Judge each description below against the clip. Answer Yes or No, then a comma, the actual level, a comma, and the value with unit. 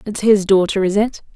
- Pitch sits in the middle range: No, high, 200 Hz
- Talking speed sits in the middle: No, fast, 220 wpm